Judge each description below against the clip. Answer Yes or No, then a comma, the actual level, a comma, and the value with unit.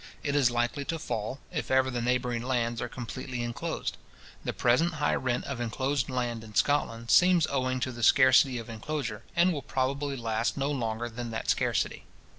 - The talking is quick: No, average, 185 wpm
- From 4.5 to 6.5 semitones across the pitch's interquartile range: No, average, 2.9 semitones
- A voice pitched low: Yes, low, 125 Hz